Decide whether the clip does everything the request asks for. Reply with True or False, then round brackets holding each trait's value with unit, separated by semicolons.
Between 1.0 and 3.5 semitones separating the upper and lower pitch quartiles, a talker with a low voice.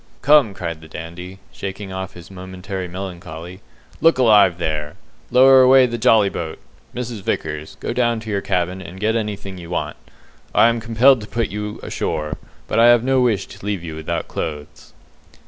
False (4.9 semitones; 95 Hz)